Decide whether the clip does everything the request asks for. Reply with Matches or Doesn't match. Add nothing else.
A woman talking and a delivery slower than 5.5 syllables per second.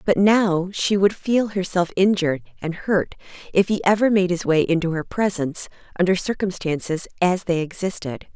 Matches